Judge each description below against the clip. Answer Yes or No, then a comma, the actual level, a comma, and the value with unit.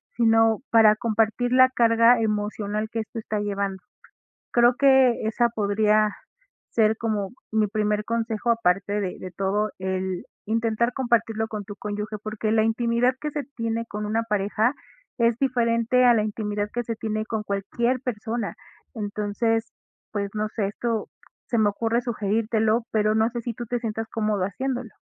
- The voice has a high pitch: Yes, high, 220 Hz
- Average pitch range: No, narrow, 1.9 semitones